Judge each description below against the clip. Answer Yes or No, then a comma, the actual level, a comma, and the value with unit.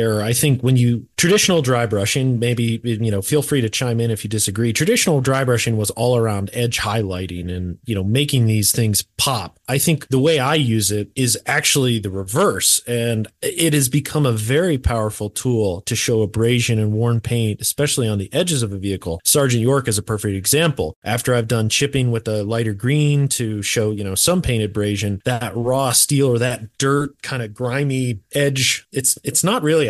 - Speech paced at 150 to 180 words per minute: No, average, 200 wpm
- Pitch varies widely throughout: No, average, 4.0 semitones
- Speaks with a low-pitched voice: Yes, low, 120 Hz